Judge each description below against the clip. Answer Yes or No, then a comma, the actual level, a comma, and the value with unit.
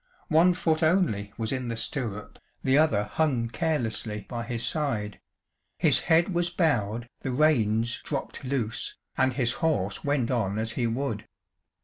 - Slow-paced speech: No, average, 150 wpm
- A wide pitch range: Yes, wide, 5.7 semitones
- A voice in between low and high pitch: No, low, 125 Hz